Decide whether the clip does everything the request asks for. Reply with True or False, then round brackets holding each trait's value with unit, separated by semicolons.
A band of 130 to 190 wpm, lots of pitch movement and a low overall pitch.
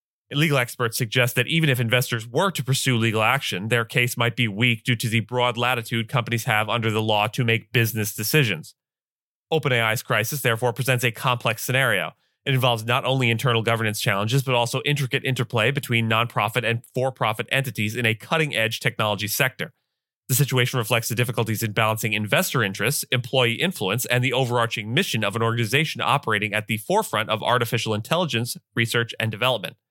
False (180 wpm; 2.4 semitones; 120 Hz)